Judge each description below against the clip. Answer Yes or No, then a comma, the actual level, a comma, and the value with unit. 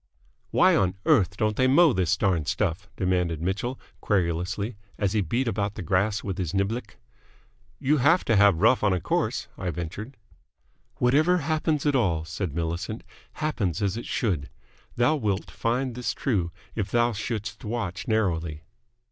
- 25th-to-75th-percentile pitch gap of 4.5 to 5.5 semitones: Yes, average, 5.0 semitones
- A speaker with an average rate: Yes, average, 160 wpm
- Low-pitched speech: Yes, low, 105 Hz